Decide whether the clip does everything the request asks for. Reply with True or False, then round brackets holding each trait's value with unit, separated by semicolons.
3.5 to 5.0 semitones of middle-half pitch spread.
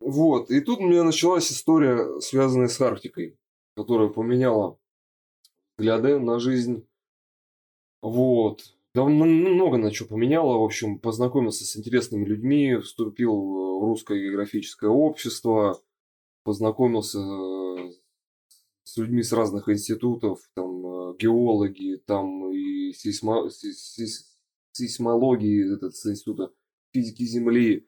True (3.8 semitones)